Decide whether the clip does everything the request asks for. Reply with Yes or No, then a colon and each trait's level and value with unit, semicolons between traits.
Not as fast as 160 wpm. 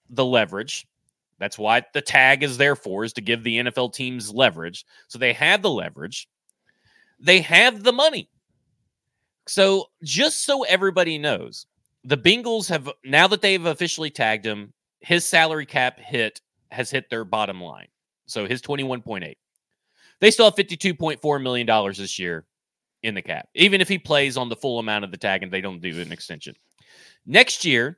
No: average, 175 wpm